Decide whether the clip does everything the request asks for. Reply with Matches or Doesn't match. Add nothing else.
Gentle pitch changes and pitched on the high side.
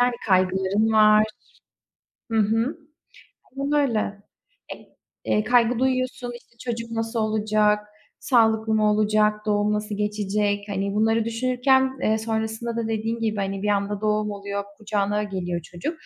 Matches